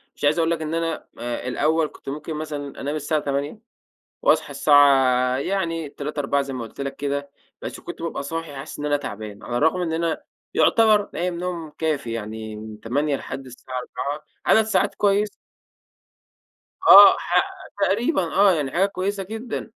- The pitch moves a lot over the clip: No, average, 3.7 semitones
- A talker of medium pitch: Yes, medium, 150 Hz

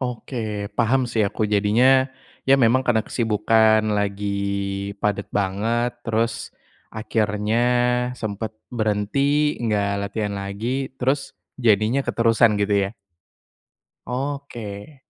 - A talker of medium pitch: No, low, 110 Hz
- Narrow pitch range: No, average, 3.0 semitones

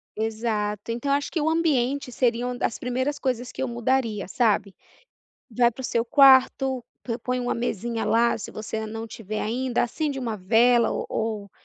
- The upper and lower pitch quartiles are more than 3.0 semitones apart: No, average, 2.7 semitones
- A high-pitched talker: Yes, high, 240 Hz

